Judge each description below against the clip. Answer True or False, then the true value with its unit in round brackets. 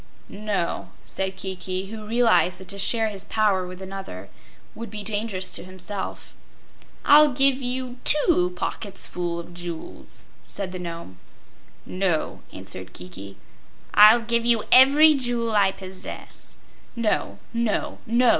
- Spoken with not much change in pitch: False (4.2 semitones)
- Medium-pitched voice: False (200 Hz)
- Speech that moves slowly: True (130 wpm)